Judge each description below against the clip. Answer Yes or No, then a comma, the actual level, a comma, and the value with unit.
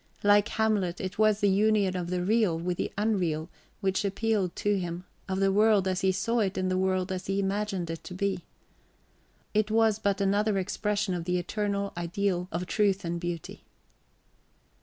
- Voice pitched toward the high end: Yes, high, 195 Hz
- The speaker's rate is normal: Yes, average, 180 wpm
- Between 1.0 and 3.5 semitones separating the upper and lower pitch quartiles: Yes, narrow, 2.4 semitones